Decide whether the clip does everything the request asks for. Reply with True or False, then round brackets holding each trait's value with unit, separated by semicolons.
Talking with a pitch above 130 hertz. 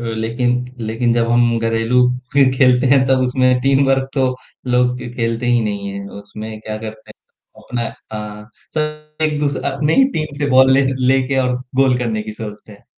False (125 Hz)